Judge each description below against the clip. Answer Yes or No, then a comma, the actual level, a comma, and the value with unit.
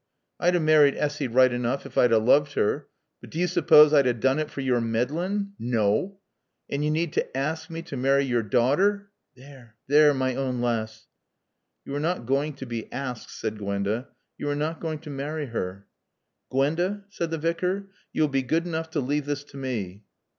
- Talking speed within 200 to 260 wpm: Yes, fast, 205 wpm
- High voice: No, medium, 140 Hz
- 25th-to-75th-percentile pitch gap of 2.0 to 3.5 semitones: No, average, 4.5 semitones